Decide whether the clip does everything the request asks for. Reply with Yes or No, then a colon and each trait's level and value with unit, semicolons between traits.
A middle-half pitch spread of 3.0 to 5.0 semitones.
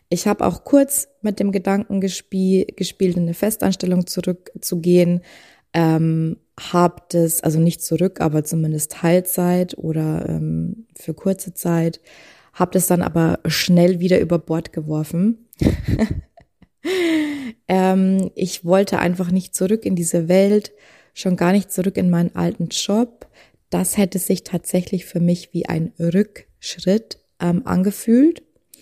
No: narrow, 2.4 semitones